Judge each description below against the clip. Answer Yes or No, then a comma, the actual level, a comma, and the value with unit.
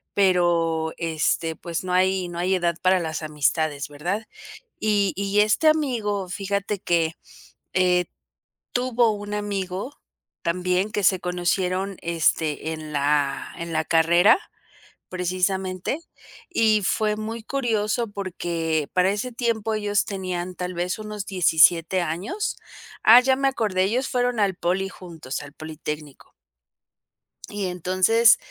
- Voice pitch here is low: No, medium, 185 Hz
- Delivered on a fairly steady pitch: No, average, 3.6 semitones